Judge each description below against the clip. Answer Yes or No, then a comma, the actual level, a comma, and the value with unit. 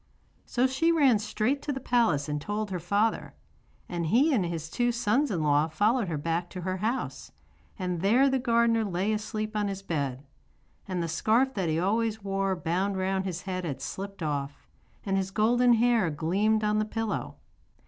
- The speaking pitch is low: No, high, 200 Hz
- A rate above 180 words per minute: Yes, average, 190 wpm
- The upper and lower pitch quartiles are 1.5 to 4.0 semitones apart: No, average, 4.7 semitones